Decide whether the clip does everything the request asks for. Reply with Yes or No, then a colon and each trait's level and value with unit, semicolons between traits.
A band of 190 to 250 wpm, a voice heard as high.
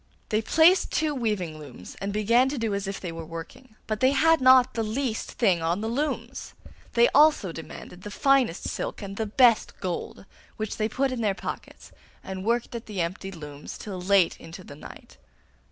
Yes: average, 195 wpm; high, 215 Hz